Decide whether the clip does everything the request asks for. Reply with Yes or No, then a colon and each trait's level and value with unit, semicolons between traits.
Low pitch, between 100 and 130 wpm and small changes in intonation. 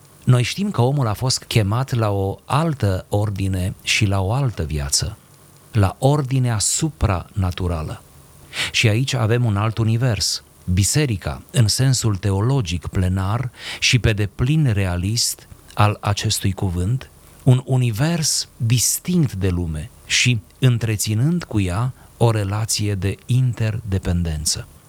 No: low, 110 Hz; average, 120 wpm; average, 4.7 semitones